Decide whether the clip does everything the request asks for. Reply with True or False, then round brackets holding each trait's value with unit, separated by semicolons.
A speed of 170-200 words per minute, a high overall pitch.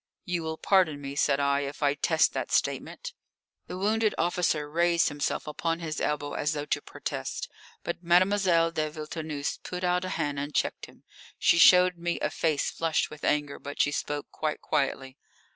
False (180 wpm; 155 Hz)